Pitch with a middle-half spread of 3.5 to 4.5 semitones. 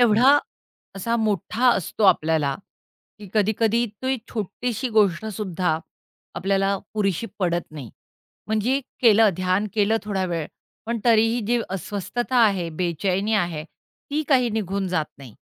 Yes: average, 4.0 semitones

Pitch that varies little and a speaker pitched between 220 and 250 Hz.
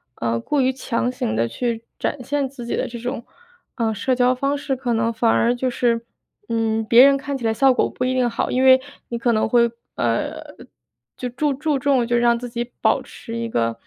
Yes: narrow, 2.1 semitones; high, 240 Hz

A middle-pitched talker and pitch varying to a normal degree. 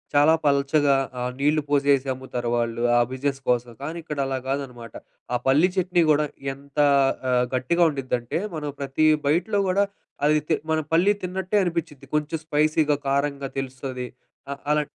Yes: medium, 145 Hz; average, 3.0 semitones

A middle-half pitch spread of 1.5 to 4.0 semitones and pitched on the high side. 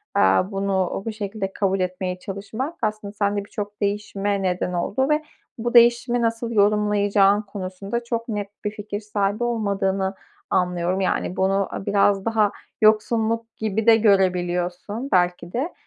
Yes: narrow, 2.4 semitones; high, 205 Hz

